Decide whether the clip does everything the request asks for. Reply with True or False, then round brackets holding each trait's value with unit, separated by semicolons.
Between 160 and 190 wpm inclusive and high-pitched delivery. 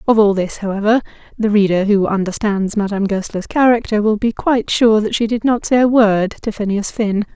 False (205 wpm; 210 Hz)